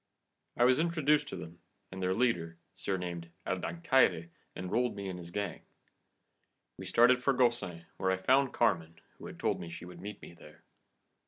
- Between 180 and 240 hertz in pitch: No, very low, 95 Hz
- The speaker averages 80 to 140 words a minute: No, average, 175 wpm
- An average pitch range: No, wide, 6.4 semitones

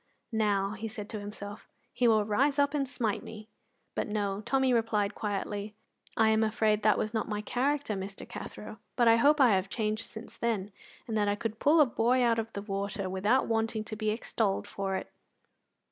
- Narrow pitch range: Yes, narrow, 2.3 semitones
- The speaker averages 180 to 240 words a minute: Yes, average, 200 wpm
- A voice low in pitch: No, high, 215 Hz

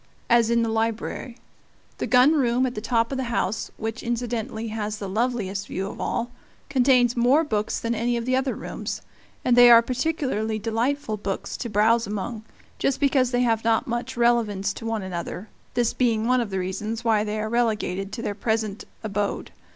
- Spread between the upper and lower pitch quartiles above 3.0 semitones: No, narrow, 2.4 semitones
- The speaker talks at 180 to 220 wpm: Yes, average, 190 wpm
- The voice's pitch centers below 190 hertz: No, high, 230 Hz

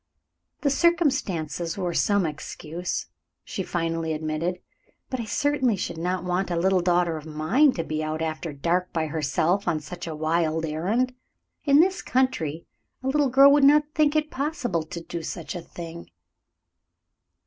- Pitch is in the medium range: Yes, medium, 175 Hz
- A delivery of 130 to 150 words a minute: No, average, 160 wpm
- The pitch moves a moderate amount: No, wide, 8.2 semitones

